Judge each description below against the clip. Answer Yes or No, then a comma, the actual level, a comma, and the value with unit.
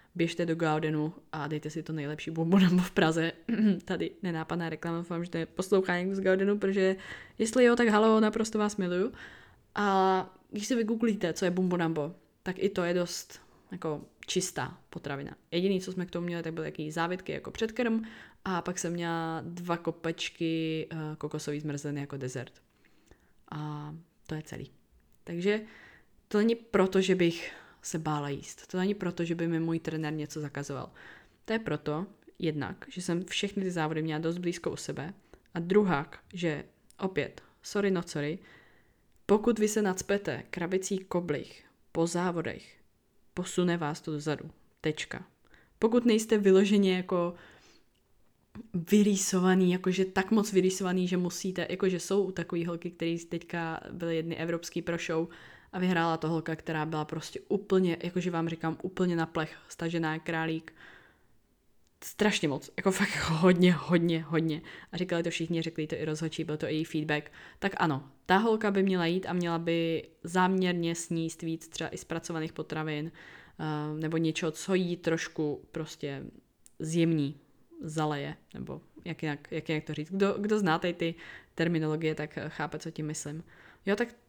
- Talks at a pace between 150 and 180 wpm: Yes, average, 160 wpm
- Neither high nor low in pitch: Yes, medium, 170 Hz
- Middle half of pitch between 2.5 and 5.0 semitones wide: Yes, average, 2.9 semitones